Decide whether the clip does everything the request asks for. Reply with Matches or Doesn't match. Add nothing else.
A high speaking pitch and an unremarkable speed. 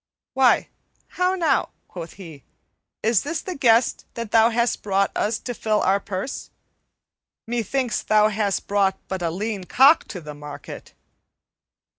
Matches